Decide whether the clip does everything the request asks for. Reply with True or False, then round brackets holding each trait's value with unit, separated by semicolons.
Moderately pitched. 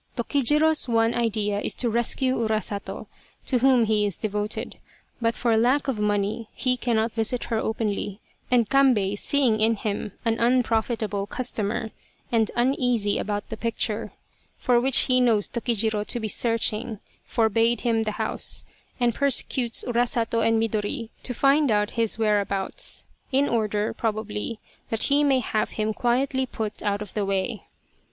False (225 Hz)